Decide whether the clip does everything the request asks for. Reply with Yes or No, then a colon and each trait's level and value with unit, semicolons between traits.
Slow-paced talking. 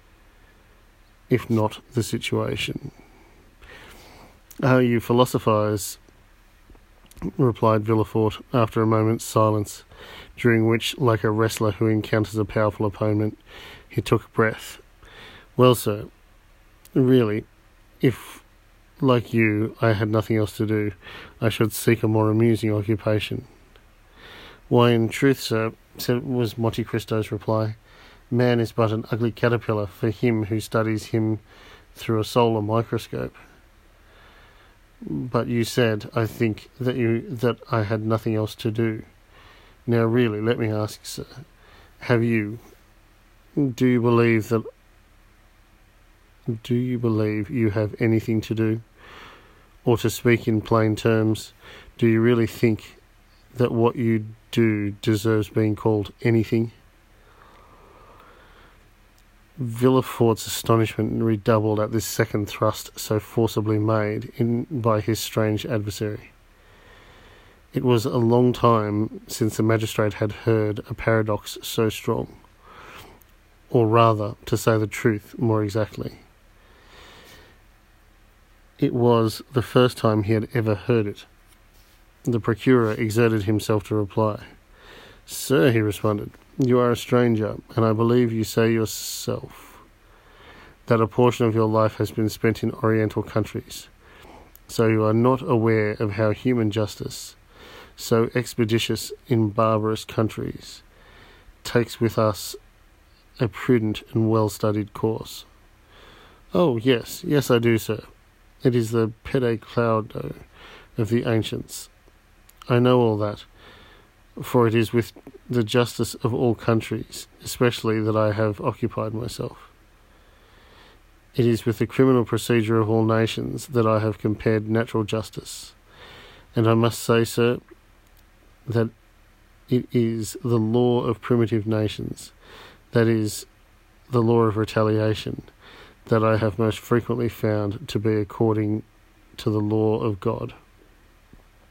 Yes: slow, 130 wpm